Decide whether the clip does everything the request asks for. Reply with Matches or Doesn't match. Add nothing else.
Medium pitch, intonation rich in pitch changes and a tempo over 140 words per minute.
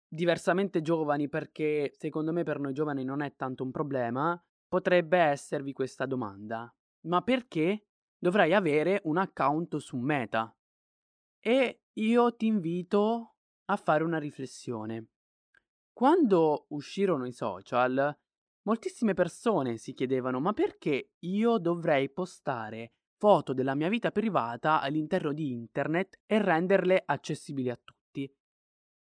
Doesn't match